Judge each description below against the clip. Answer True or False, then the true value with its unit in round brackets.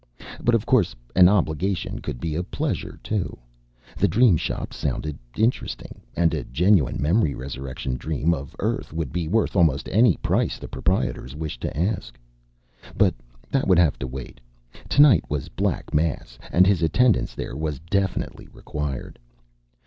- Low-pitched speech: True (80 Hz)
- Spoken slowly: False (155 wpm)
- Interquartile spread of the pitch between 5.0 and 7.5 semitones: True (5.5 semitones)